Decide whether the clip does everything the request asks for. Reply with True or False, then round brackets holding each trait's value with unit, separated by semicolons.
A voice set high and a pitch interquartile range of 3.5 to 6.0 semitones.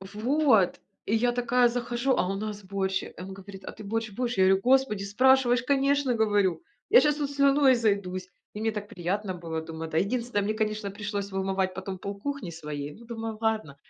True (210 Hz; 4.2 semitones)